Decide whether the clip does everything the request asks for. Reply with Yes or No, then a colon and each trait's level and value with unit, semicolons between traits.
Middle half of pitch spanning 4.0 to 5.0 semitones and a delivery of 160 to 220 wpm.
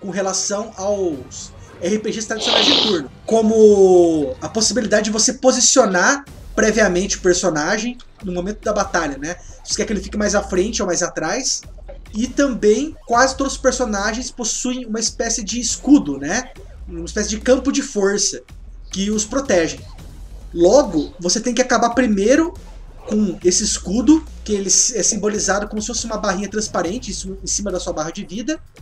Yes: average, 4.4 semitones; average, 165 wpm